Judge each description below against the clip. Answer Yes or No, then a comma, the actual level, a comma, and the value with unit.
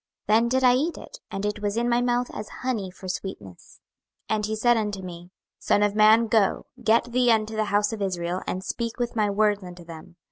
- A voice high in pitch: Yes, high, 215 Hz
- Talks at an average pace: No, fast, 225 wpm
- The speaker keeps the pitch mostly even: No, average, 3.4 semitones